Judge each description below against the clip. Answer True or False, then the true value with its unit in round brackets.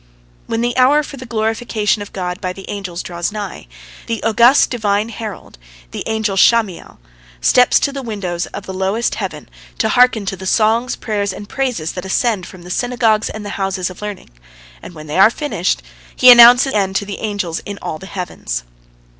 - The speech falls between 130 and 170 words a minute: False (195 wpm)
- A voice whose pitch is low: False (210 Hz)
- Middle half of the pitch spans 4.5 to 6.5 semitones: False (3.6 semitones)